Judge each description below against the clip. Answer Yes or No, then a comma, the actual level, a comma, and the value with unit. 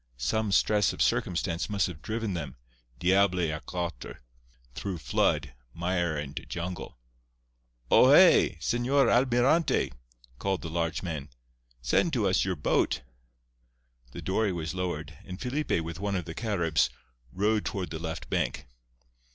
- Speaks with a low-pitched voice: Yes, very low, 90 Hz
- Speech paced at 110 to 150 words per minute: Yes, average, 140 wpm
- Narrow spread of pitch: No, average, 4.1 semitones